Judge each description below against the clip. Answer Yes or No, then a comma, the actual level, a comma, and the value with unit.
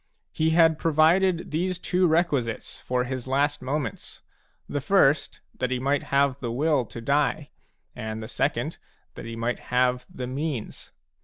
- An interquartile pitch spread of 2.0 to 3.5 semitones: No, average, 4.1 semitones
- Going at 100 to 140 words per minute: No, average, 160 wpm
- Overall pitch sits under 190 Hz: Yes, medium, 140 Hz